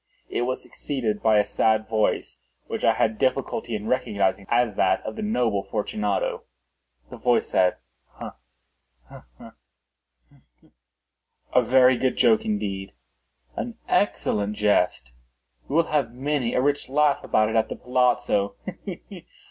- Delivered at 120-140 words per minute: Yes, slow, 135 wpm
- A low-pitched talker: Yes, low, 110 Hz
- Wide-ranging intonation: No, average, 4.1 semitones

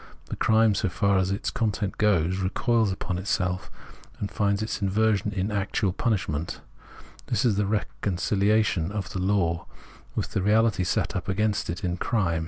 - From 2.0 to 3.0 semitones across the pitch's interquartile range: Yes, narrow, 2.5 semitones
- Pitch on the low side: Yes, low, 100 Hz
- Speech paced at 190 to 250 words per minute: No, average, 160 wpm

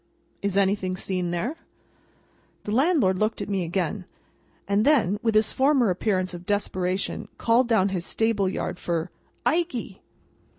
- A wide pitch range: No, average, 3.6 semitones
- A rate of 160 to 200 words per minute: No, average, 140 wpm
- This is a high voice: Yes, high, 200 Hz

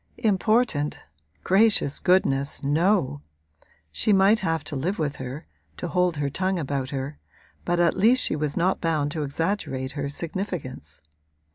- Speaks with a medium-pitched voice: Yes, medium, 160 Hz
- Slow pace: No, average, 145 wpm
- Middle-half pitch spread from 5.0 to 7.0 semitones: Yes, average, 5.3 semitones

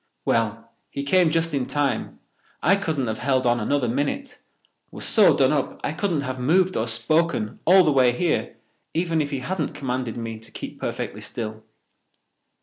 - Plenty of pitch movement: Yes, wide, 5.7 semitones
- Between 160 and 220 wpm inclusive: Yes, average, 170 wpm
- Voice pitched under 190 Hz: Yes, medium, 140 Hz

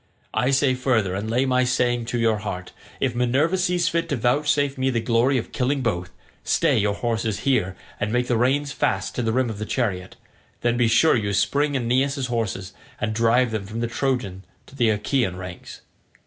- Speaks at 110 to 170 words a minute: No, average, 195 wpm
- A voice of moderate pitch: No, low, 120 Hz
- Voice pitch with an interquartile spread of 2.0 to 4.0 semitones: Yes, average, 3.4 semitones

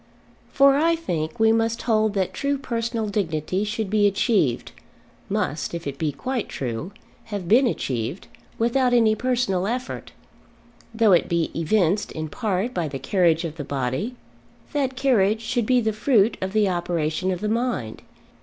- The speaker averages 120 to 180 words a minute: Yes, average, 165 wpm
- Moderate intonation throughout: No, wide, 5.8 semitones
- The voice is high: Yes, high, 210 Hz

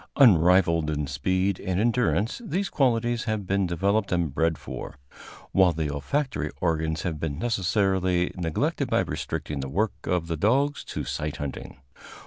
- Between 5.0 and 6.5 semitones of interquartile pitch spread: Yes, average, 5.3 semitones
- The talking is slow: No, average, 150 wpm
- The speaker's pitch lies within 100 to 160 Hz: No, very low, 90 Hz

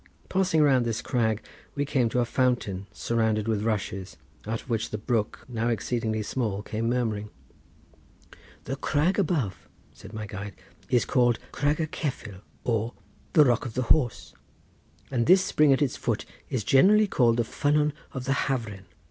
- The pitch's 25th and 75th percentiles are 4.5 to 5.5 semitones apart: No, average, 4.0 semitones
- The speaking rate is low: No, average, 165 wpm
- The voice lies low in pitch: Yes, low, 120 Hz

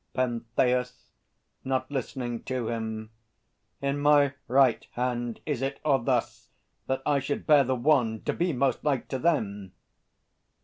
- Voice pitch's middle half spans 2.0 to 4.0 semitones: Yes, average, 2.8 semitones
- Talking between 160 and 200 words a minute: No, average, 140 wpm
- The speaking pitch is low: Yes, low, 130 Hz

